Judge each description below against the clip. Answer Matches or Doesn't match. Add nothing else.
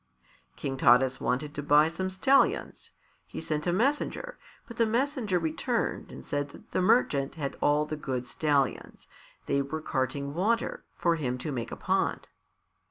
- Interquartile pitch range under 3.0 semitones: Doesn't match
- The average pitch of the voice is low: Doesn't match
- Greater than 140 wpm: Matches